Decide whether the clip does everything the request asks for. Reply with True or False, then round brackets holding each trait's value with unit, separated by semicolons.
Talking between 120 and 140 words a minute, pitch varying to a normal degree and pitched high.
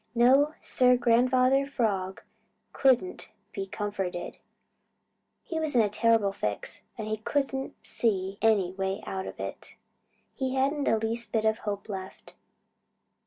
True (135 wpm; 4.6 semitones; 225 Hz)